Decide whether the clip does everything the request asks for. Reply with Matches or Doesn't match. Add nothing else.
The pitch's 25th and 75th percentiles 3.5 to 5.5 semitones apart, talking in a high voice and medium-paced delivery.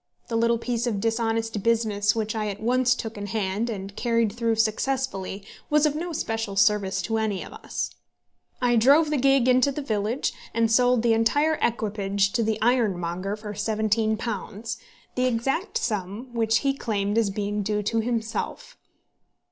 Doesn't match